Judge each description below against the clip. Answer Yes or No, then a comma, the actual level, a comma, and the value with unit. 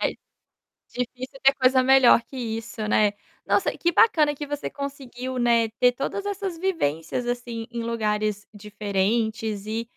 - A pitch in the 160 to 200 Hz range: No, high, 240 Hz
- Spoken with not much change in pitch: No, average, 3.7 semitones